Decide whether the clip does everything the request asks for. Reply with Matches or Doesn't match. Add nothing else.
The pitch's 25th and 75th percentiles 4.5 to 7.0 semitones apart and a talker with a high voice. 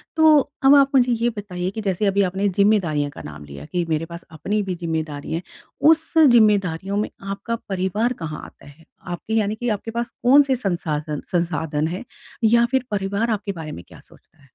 Matches